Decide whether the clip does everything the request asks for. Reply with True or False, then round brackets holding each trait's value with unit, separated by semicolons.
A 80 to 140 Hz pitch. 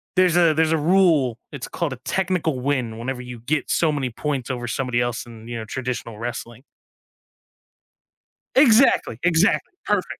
True (135 Hz)